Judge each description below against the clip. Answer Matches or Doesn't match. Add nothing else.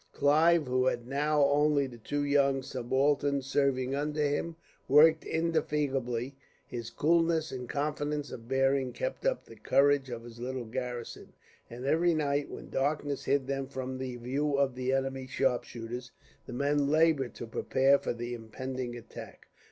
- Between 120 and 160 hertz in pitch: Matches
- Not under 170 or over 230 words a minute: Doesn't match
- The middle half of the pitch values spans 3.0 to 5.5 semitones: Doesn't match